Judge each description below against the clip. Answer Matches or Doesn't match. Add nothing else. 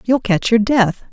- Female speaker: Matches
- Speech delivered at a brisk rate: Matches